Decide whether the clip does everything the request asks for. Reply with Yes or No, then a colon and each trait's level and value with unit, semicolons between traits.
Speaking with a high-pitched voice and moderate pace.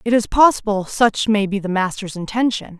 Yes: high, 210 Hz; average, 195 wpm